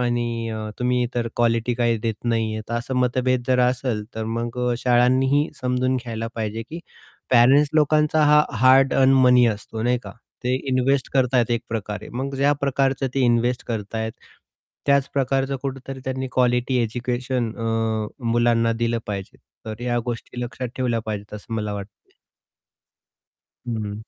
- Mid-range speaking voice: No, low, 120 Hz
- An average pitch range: No, narrow, 2.3 semitones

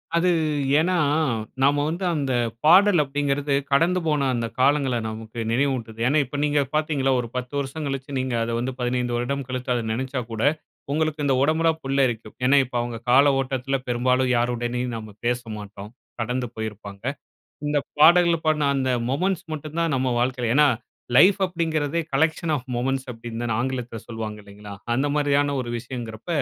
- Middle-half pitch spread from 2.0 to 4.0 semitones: Yes, average, 3.6 semitones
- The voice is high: No, low, 130 Hz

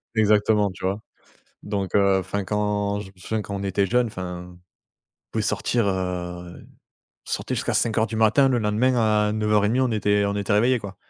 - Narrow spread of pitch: Yes, narrow, 2.1 semitones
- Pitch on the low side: Yes, low, 105 Hz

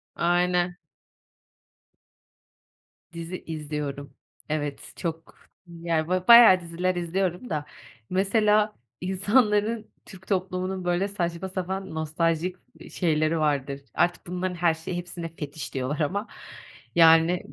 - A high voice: No, medium, 175 Hz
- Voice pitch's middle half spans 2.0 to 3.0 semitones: Yes, narrow, 2.5 semitones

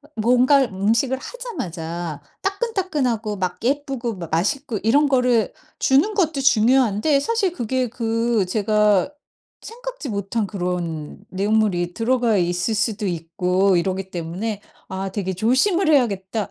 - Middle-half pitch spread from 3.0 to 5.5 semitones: No, wide, 6.1 semitones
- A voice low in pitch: No, high, 225 Hz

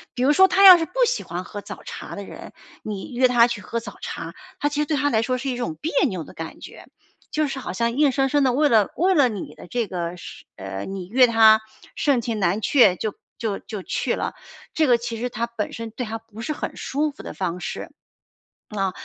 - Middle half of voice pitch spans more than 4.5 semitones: Yes, average, 5.1 semitones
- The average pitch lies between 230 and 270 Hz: Yes, high, 235 Hz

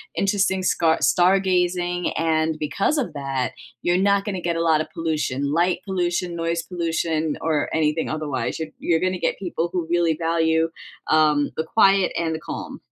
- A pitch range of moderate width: No, narrow, 2.3 semitones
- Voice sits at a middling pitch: Yes, medium, 165 Hz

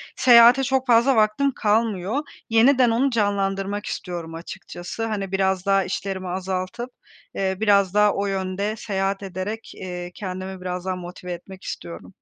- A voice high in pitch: Yes, high, 195 Hz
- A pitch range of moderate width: Yes, average, 3.2 semitones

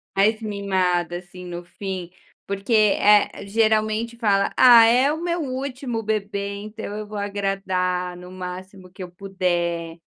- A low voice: No, high, 200 Hz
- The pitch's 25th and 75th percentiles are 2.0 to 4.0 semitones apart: Yes, average, 3.1 semitones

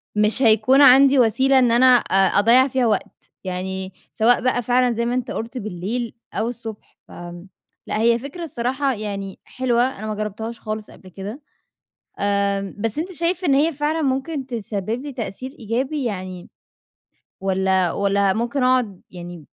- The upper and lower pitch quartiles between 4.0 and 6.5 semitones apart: Yes, average, 4.5 semitones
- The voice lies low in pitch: No, high, 230 Hz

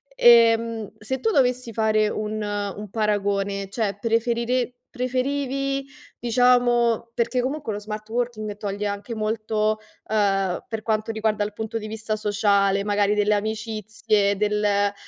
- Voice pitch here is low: No, high, 215 Hz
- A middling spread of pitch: No, narrow, 2.2 semitones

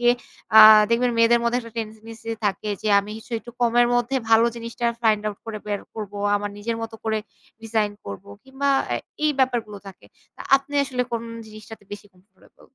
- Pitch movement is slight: Yes, narrow, 2.1 semitones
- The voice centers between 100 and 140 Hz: No, high, 225 Hz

